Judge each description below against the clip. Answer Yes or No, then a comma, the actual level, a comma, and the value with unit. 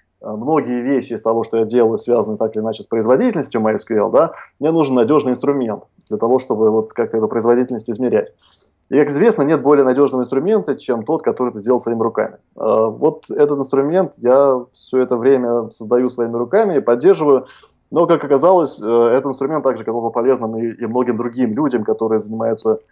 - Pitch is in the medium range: No, low, 125 Hz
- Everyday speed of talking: No, fast, 175 wpm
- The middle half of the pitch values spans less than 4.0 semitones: Yes, average, 3.4 semitones